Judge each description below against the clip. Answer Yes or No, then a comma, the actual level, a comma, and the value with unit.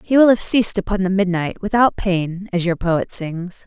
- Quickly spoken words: Yes, fast, 215 wpm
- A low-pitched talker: No, high, 190 Hz